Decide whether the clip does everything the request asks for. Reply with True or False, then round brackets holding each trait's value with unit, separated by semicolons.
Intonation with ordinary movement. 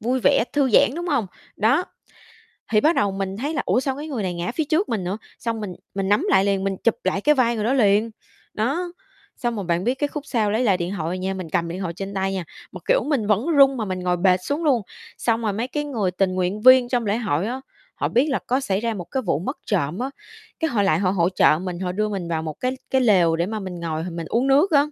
False (5.7 semitones)